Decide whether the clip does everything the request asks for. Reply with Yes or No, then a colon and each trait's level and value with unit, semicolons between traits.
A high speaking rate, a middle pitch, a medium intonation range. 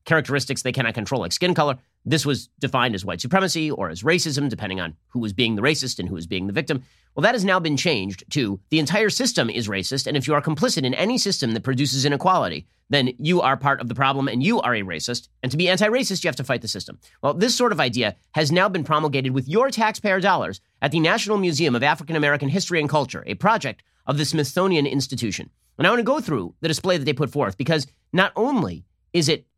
Yes: fast, 245 wpm; medium, 145 Hz; average, 5.0 semitones